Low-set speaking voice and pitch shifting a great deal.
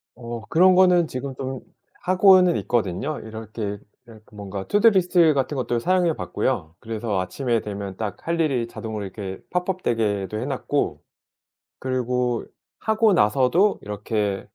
Yes: low, 120 Hz; wide, 8.3 semitones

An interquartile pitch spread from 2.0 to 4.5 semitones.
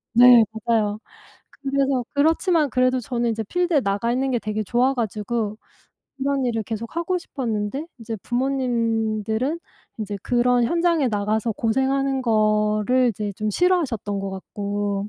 Yes: average, 4.0 semitones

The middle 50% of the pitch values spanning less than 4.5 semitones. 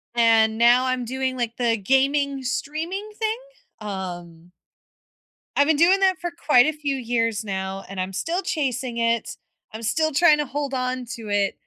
No: average, 5.0 semitones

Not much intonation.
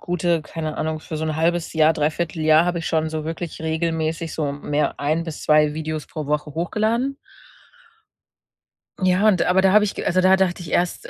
Yes: narrow, 2.2 semitones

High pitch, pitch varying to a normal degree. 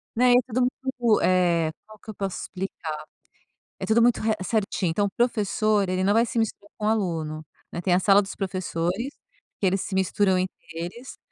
Yes: high, 195 Hz; average, 3.2 semitones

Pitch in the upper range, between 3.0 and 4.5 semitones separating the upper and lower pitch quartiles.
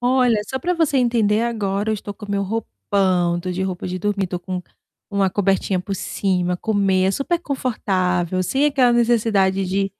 Yes: high, 200 Hz; average, 4.0 semitones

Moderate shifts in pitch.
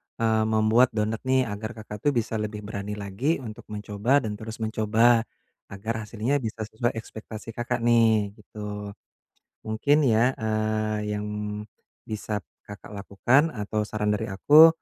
No: narrow, 1.8 semitones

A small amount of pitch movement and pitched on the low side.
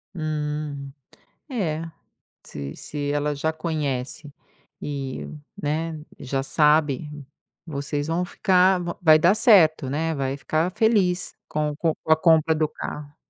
No: narrow, 2.2 semitones; medium, 155 Hz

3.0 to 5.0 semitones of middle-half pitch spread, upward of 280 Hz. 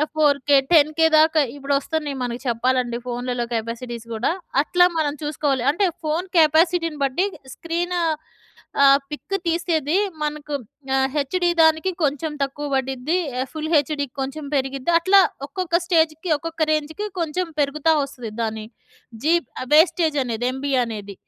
Yes: average, 3.6 semitones; very high, 300 Hz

